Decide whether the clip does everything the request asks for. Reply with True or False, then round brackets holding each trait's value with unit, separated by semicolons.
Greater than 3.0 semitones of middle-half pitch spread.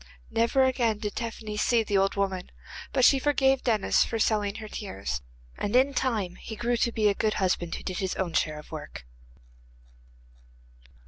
True (3.8 semitones)